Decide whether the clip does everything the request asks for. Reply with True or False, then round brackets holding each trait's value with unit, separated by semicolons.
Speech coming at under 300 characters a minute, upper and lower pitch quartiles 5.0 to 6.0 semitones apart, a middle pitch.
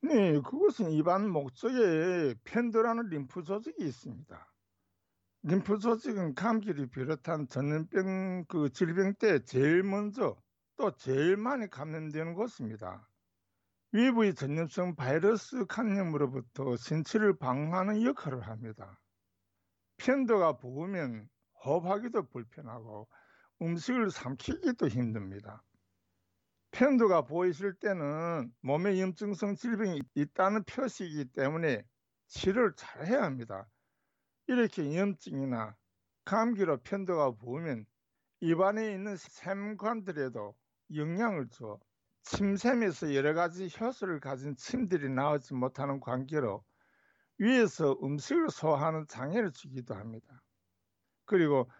False (260 characters per minute; 8.1 semitones; 155 Hz)